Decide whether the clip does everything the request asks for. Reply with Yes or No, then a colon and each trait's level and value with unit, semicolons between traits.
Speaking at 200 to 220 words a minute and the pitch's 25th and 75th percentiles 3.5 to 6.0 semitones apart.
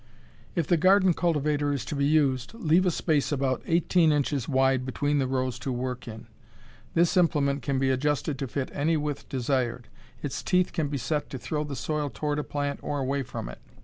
No: fast, 205 wpm; average, 2.7 semitones